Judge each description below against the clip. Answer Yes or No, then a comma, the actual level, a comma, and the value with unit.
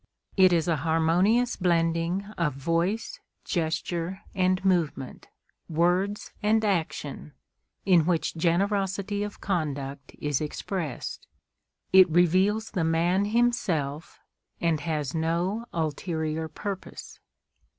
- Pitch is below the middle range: No, medium, 170 Hz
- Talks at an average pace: No, slow, 100 wpm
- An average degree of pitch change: Yes, average, 3.3 semitones